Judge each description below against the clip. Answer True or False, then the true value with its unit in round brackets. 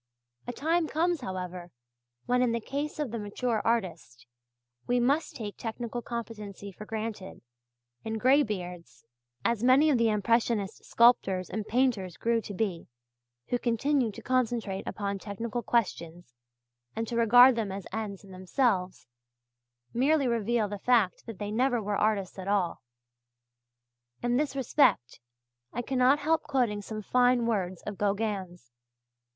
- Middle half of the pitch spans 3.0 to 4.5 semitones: True (3.7 semitones)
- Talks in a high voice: True (225 Hz)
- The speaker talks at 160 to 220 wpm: False (145 wpm)